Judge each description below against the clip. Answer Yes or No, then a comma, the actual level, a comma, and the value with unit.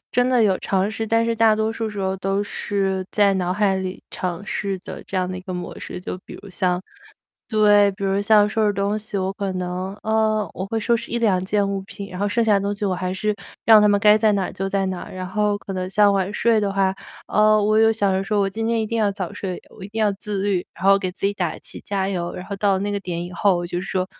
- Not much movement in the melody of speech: Yes, narrow, 2.1 semitones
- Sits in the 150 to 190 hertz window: No, high, 200 Hz